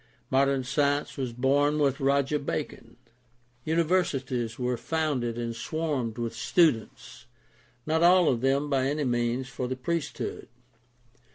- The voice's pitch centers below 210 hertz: Yes, low, 135 Hz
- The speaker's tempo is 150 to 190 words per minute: No, slow, 135 wpm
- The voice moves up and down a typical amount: Yes, average, 3.3 semitones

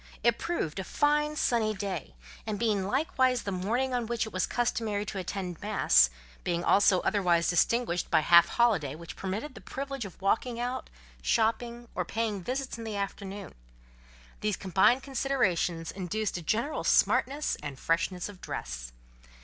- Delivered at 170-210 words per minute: No, average, 160 wpm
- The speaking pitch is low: No, high, 205 Hz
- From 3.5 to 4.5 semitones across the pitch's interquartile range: No, average, 4.9 semitones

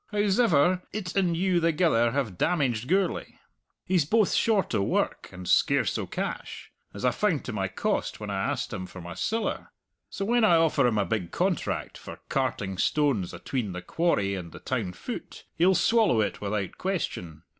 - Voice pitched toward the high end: No, medium, 140 Hz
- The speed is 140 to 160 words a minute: No, average, 180 wpm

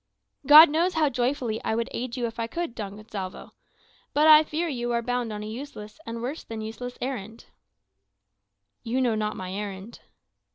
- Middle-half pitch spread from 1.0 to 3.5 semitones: No, average, 4.0 semitones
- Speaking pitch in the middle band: No, high, 235 Hz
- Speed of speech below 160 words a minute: No, average, 180 wpm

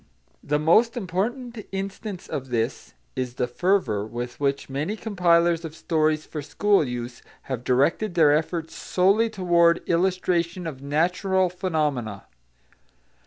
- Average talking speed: No, slow, 125 wpm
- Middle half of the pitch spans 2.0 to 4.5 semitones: No, average, 5.2 semitones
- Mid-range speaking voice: Yes, medium, 170 Hz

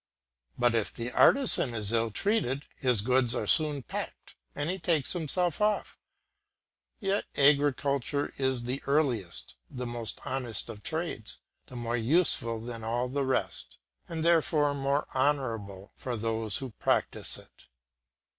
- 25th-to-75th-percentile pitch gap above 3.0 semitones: Yes, average, 4.2 semitones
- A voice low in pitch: Yes, low, 130 Hz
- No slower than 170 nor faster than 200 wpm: No, average, 140 wpm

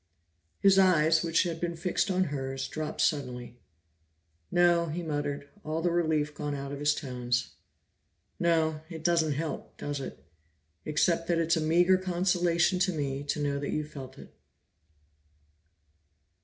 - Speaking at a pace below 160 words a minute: Yes, average, 150 wpm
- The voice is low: No, medium, 160 Hz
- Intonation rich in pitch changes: No, average, 3.1 semitones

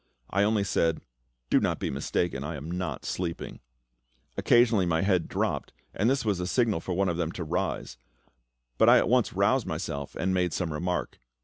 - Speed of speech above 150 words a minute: Yes, average, 190 wpm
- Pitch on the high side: No, very low, 90 Hz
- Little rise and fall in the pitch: No, average, 3.3 semitones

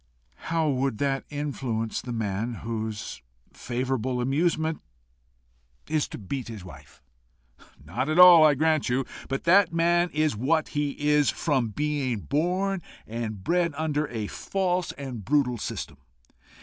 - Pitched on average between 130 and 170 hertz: Yes, medium, 140 Hz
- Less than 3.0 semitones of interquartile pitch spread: No, average, 5.0 semitones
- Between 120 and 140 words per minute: Yes, slow, 135 wpm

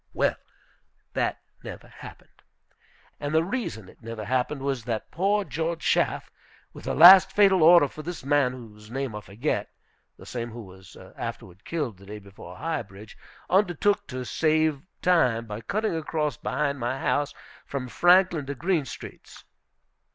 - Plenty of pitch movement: Yes, wide, 6.4 semitones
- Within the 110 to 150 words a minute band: No, average, 160 wpm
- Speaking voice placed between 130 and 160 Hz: Yes, medium, 140 Hz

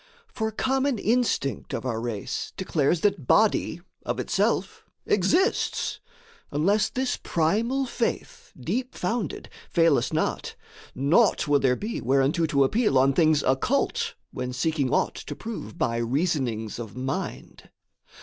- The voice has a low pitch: No, medium, 160 Hz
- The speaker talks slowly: Yes, slow, 130 wpm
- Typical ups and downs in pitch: No, wide, 8.7 semitones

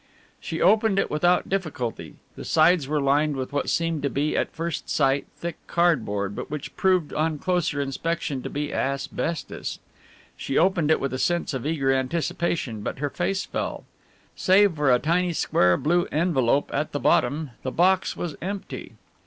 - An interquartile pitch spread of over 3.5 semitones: Yes, average, 4.0 semitones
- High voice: No, medium, 155 Hz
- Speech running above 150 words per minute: Yes, average, 170 wpm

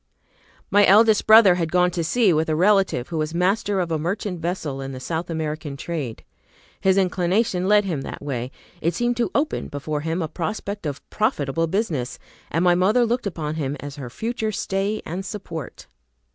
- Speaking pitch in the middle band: Yes, medium, 175 Hz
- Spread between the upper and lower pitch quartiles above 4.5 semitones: Yes, average, 4.9 semitones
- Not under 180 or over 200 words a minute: Yes, average, 185 wpm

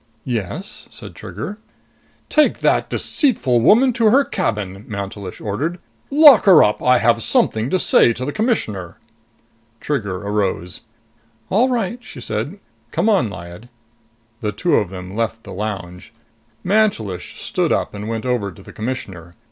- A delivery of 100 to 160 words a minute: Yes, average, 150 wpm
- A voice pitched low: Yes, low, 115 Hz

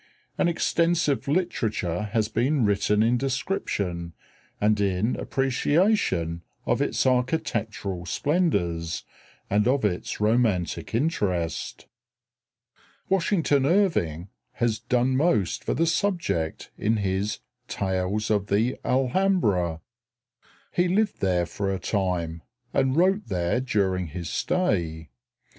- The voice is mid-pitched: No, low, 110 Hz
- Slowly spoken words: Yes, slow, 110 wpm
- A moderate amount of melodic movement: No, wide, 7.4 semitones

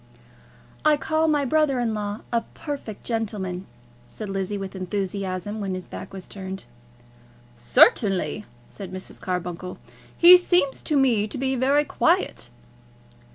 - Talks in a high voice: Yes, high, 210 Hz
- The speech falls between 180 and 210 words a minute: No, slow, 135 wpm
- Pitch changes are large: Yes, wide, 6.1 semitones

